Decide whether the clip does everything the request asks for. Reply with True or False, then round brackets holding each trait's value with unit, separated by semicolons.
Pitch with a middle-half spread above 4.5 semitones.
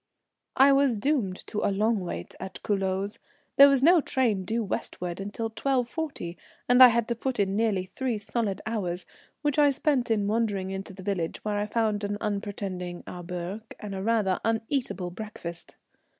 False (3.7 semitones)